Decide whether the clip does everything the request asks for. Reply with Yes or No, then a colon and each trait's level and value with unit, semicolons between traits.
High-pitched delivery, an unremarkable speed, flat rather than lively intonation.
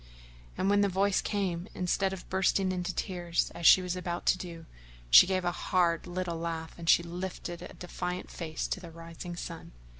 No: medium, 180 Hz; average, 190 wpm; narrow, 1.6 semitones